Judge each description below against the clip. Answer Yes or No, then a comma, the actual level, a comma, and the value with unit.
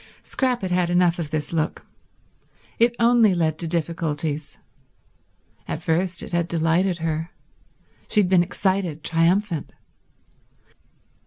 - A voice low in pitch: No, medium, 170 Hz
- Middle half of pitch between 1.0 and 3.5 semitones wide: Yes, average, 2.7 semitones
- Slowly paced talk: Yes, slow, 125 wpm